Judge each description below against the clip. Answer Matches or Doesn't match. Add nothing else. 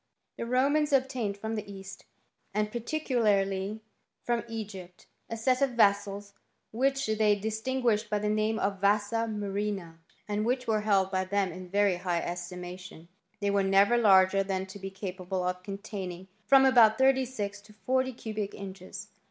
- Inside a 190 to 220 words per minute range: Doesn't match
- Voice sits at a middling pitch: Doesn't match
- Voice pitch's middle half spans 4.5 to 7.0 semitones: Doesn't match